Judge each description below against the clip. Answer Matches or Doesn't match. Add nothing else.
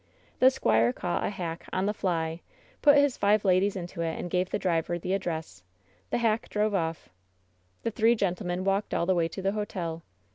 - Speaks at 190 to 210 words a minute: Matches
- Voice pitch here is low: Doesn't match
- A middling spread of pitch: Matches